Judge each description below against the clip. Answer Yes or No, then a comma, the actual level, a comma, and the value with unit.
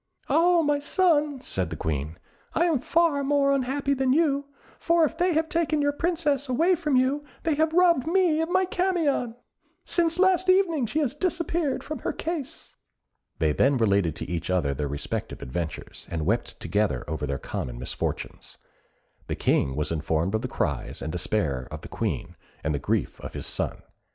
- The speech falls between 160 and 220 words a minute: Yes, average, 180 wpm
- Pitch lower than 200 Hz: No, very high, 280 Hz